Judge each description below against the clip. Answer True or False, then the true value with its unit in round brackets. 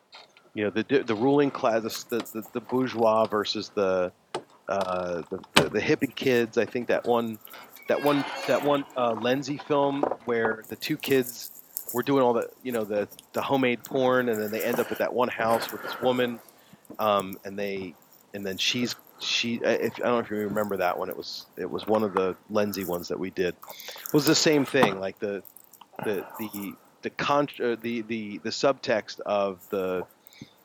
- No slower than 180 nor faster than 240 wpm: True (200 wpm)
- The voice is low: True (115 Hz)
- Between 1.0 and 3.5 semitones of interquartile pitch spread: False (4.0 semitones)